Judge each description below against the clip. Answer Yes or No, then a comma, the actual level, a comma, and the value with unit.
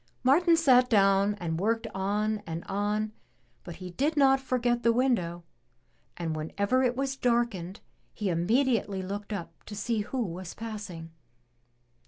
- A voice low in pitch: No, high, 210 Hz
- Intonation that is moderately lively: Yes, average, 4.9 semitones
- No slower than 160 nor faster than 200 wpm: No, average, 145 wpm